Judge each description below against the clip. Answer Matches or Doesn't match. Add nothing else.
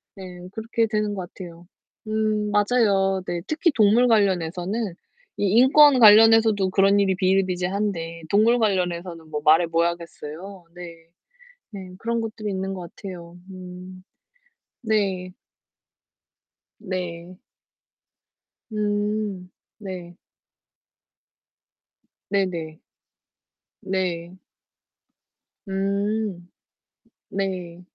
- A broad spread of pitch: Doesn't match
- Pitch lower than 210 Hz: Matches